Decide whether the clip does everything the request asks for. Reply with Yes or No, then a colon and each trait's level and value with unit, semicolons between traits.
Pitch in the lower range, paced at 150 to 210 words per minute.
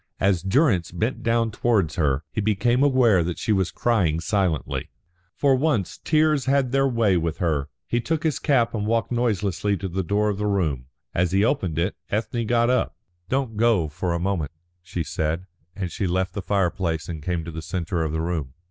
Yes: low, 100 Hz; average, 200 wpm